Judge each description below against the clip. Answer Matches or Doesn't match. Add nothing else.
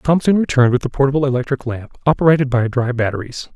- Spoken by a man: Matches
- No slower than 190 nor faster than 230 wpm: Matches